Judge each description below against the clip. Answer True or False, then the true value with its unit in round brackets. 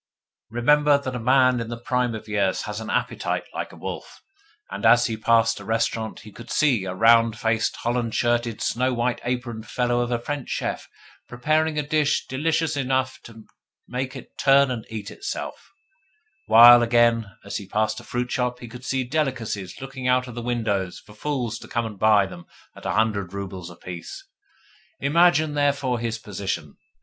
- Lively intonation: False (2.9 semitones)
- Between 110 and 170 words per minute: False (185 wpm)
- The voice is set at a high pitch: False (120 Hz)